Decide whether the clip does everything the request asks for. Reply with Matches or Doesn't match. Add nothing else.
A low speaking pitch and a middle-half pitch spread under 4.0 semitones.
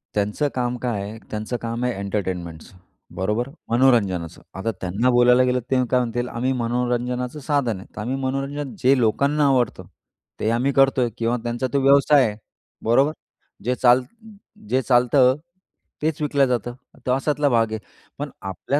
Matches